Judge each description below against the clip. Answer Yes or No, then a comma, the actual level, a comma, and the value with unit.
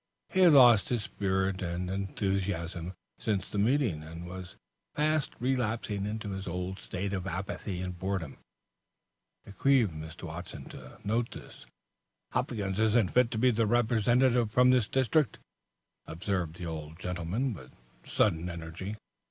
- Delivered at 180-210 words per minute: No, average, 145 wpm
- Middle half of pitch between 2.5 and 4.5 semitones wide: No, average, 4.9 semitones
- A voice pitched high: No, low, 100 Hz